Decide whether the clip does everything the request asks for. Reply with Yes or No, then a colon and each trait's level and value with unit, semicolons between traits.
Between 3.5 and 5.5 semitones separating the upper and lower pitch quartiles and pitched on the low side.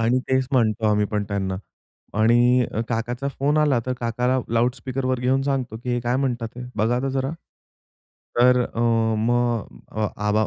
No: narrow, 2.5 semitones; low, 120 Hz